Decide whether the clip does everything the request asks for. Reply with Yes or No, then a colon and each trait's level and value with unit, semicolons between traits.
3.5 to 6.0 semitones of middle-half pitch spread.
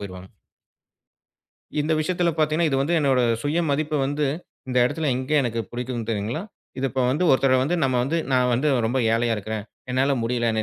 Yes: average, 4.1 semitones